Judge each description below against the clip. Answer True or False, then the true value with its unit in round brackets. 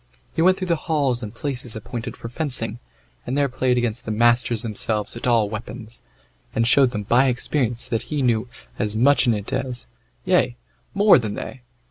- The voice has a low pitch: True (120 Hz)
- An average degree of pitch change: True (3.0 semitones)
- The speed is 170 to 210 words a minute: True (185 wpm)